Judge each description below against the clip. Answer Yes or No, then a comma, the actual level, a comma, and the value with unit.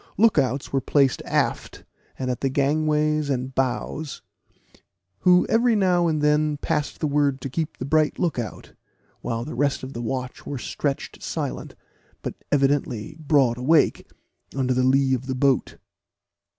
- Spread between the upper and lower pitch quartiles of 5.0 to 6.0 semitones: No, average, 2.8 semitones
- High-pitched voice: No, medium, 140 Hz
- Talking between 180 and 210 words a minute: No, average, 160 wpm